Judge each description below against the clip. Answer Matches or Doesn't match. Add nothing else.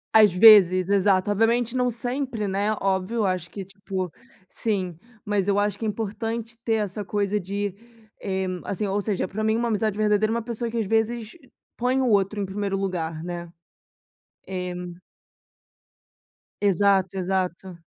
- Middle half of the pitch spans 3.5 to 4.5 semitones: Doesn't match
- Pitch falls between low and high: Doesn't match